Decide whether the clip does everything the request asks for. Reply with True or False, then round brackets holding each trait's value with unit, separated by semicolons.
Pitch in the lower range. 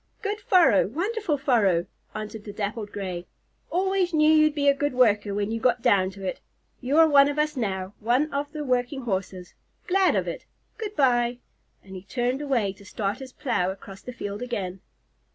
False (245 Hz)